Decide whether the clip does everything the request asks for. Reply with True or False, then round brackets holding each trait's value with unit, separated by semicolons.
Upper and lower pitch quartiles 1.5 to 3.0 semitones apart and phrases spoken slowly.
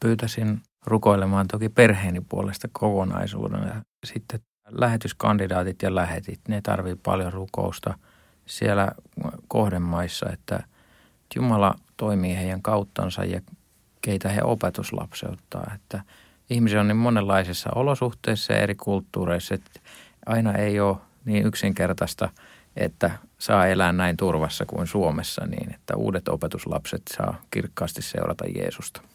False (2.7 semitones; 115 wpm)